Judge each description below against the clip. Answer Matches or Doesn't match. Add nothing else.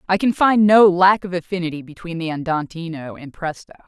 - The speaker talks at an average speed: Matches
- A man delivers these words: Doesn't match